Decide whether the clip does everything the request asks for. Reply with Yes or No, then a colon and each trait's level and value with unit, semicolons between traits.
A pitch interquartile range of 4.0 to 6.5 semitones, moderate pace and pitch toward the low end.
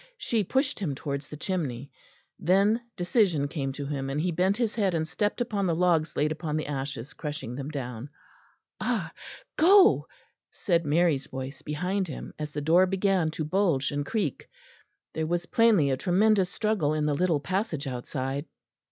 No: average, 5.1 semitones; average, 170 wpm; medium, 160 Hz